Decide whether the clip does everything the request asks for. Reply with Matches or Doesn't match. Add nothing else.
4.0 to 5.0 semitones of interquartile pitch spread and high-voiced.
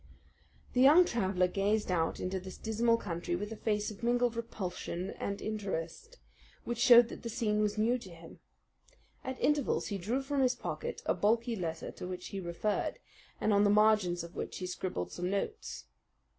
Matches